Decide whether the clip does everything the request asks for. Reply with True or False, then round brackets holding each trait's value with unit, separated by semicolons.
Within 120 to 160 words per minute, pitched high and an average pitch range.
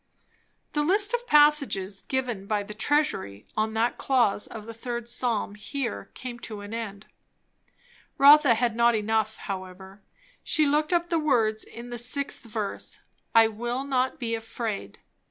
True (155 wpm; 235 Hz; 4.3 semitones)